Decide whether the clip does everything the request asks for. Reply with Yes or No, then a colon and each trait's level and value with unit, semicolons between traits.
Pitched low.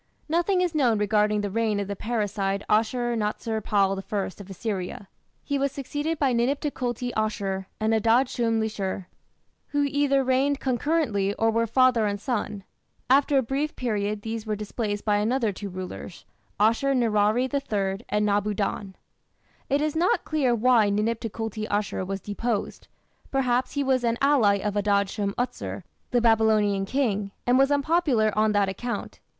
No: high, 225 Hz